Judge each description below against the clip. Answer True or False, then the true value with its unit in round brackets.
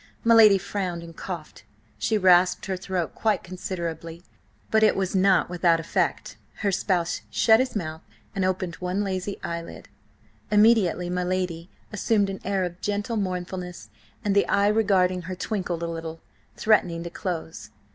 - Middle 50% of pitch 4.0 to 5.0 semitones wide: False (2.6 semitones)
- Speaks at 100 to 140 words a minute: False (155 wpm)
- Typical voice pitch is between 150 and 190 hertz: True (185 Hz)